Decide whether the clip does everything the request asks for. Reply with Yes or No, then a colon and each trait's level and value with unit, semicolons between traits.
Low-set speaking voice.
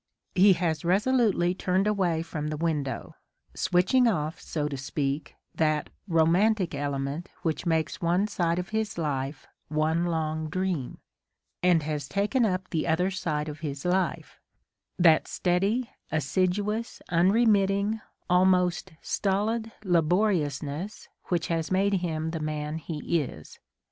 No: medium, 170 Hz